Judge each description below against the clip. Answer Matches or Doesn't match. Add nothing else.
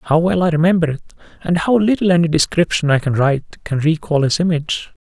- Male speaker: Matches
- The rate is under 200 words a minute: Doesn't match